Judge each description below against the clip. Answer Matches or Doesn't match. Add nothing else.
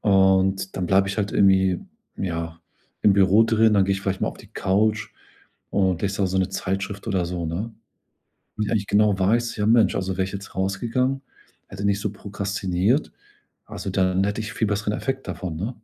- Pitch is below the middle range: Matches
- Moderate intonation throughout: Doesn't match